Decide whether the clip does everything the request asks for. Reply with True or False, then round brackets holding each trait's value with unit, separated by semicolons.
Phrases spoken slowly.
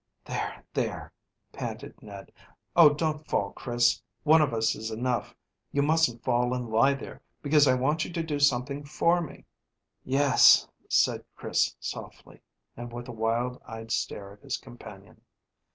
False (155 wpm)